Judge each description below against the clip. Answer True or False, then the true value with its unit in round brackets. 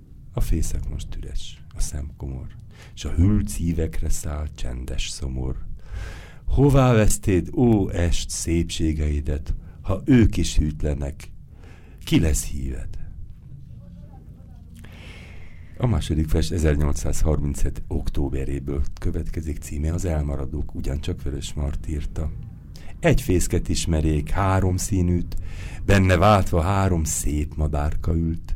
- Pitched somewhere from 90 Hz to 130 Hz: False (80 Hz)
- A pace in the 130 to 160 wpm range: False (105 wpm)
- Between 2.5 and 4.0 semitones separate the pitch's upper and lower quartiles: True (3.0 semitones)